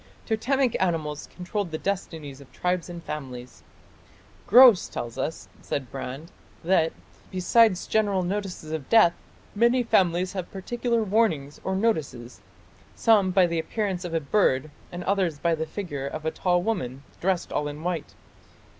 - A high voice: No, medium, 175 Hz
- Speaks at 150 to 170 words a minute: Yes, average, 155 wpm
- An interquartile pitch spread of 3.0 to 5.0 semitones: Yes, average, 4.7 semitones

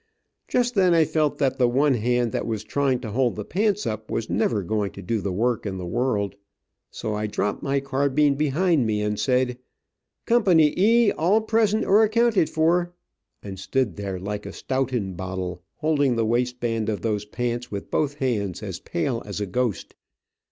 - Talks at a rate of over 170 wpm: Yes, average, 185 wpm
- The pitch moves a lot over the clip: Yes, wide, 6.4 semitones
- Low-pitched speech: Yes, low, 125 Hz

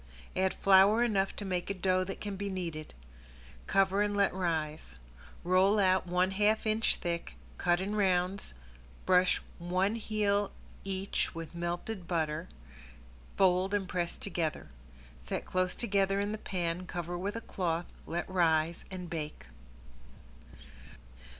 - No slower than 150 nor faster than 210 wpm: No, slow, 135 wpm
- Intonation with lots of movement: No, narrow, 2.4 semitones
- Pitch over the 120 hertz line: Yes, medium, 185 Hz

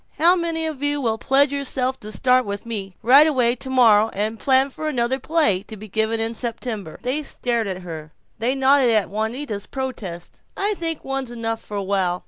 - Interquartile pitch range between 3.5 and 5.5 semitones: Yes, average, 4.2 semitones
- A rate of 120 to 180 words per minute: No, average, 200 wpm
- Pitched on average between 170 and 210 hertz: No, high, 240 Hz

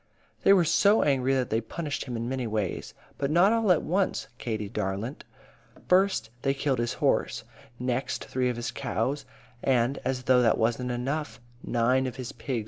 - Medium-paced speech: Yes, average, 185 wpm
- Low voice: Yes, low, 130 Hz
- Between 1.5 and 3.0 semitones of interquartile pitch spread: No, average, 3.6 semitones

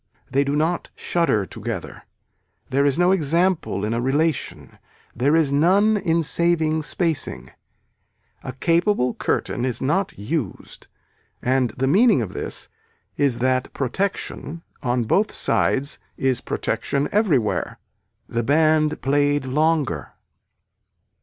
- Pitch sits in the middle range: Yes, medium, 145 Hz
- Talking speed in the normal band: No, slow, 120 wpm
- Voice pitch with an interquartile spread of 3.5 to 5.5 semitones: Yes, average, 4.4 semitones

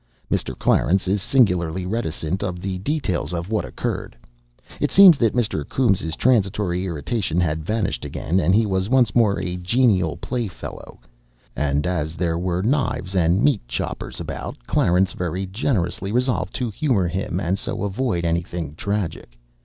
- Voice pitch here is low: Yes, very low, 95 Hz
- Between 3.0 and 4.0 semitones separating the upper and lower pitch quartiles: No, average, 4.4 semitones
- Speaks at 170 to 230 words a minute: No, average, 155 wpm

